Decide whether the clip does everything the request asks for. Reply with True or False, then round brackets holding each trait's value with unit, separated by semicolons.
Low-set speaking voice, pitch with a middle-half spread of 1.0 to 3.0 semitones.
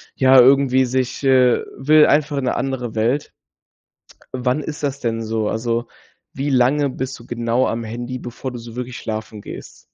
True (125 Hz; 2.4 semitones)